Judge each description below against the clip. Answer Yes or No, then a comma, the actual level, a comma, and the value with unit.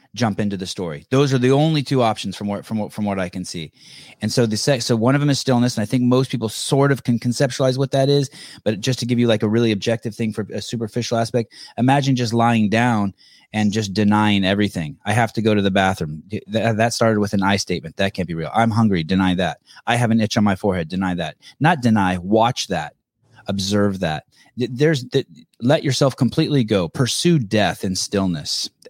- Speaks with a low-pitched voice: Yes, low, 115 Hz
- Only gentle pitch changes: No, average, 3.9 semitones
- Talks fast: Yes, fast, 225 wpm